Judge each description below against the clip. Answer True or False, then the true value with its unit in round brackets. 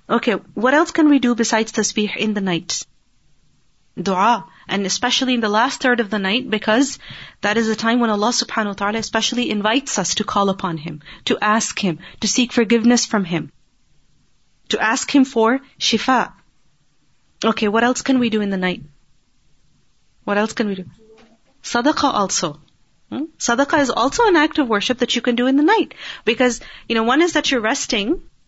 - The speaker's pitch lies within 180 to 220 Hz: False (230 Hz)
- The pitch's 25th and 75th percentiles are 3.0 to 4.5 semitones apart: True (3.5 semitones)